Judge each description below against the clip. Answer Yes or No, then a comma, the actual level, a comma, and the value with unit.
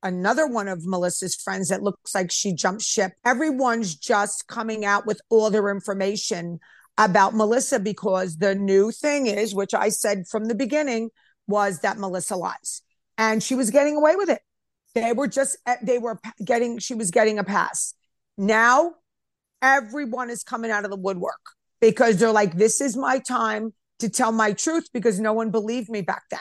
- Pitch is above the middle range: Yes, high, 220 Hz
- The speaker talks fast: No, average, 180 wpm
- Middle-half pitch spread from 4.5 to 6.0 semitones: No, average, 3.5 semitones